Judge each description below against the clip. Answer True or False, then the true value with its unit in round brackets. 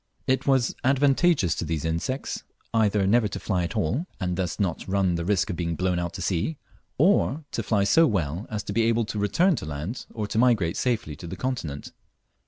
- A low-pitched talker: True (100 Hz)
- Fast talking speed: True (215 wpm)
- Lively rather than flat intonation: True (6.2 semitones)